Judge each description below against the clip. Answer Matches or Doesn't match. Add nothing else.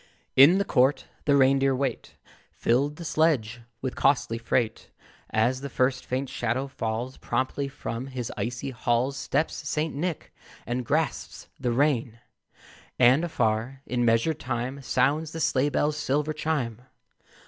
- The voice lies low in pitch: Matches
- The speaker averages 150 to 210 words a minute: Doesn't match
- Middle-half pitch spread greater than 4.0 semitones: Doesn't match